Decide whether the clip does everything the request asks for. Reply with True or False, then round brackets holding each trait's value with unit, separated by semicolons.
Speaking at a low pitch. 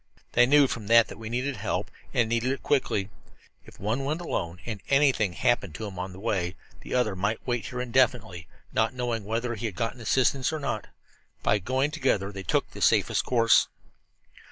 True (115 Hz)